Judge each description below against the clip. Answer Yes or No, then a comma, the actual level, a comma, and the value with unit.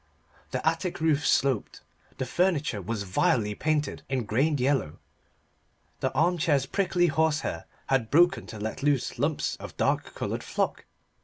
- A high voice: No, medium, 140 Hz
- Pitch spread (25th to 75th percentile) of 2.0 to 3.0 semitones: No, average, 5.2 semitones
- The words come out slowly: No, average, 145 wpm